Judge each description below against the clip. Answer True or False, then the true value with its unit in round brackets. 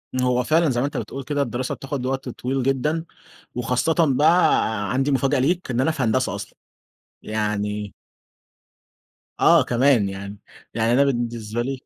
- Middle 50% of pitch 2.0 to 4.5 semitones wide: True (3.1 semitones)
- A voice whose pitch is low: True (125 Hz)